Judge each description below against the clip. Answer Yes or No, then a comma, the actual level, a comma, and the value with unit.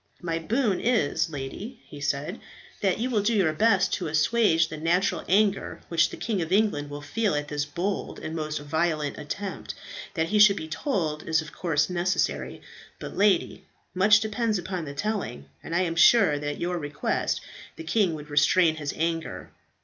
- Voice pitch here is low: No, medium, 170 Hz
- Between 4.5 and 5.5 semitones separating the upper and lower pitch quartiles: Yes, average, 5.0 semitones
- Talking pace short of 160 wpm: No, average, 185 wpm